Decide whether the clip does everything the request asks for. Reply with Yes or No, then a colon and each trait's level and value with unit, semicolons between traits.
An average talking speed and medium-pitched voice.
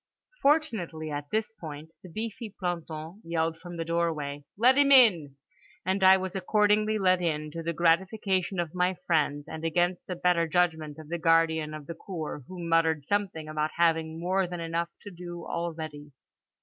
Yes: average, 175 wpm; medium, 170 Hz